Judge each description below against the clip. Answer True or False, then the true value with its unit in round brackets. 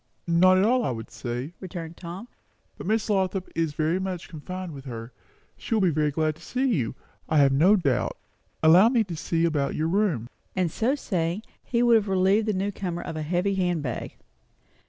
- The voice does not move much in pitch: False (4.2 semitones)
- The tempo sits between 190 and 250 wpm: True (200 wpm)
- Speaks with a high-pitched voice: False (175 Hz)